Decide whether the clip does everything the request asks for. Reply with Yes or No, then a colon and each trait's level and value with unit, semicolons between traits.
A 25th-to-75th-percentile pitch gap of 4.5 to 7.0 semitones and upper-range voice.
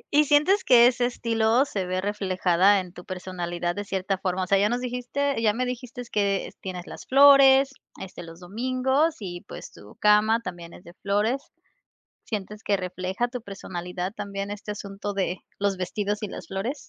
Yes: average, 4.8 semitones; high, 205 Hz